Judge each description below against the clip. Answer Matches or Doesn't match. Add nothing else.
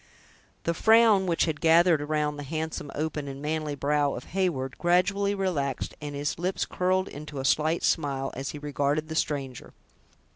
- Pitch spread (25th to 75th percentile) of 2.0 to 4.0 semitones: Matches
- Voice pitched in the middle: Matches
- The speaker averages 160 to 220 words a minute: Matches